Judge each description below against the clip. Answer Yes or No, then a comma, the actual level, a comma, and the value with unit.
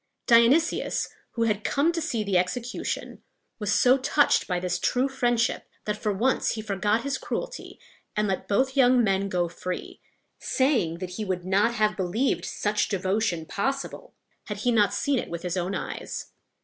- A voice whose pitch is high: Yes, high, 215 Hz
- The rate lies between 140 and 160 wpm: No, average, 175 wpm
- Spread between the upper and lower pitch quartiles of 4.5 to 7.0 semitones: Yes, average, 5.1 semitones